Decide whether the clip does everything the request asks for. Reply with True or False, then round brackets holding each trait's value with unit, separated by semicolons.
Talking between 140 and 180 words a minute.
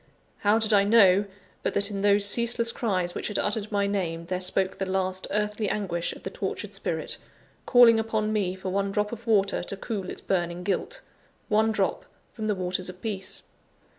False (195 wpm)